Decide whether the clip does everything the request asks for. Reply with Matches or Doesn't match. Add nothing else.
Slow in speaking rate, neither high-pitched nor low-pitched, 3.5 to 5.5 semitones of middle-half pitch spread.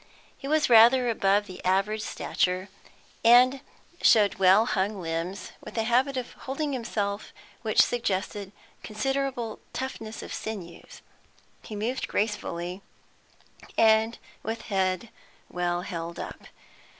Doesn't match